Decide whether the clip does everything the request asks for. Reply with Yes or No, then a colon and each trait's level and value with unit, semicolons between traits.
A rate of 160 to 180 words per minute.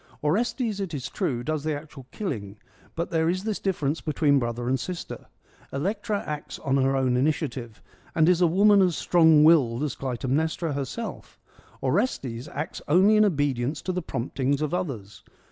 Yes: average, 170 wpm